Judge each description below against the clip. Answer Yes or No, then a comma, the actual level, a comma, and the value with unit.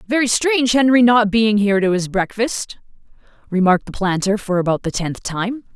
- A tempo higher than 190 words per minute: No, average, 175 wpm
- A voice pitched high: Yes, high, 210 Hz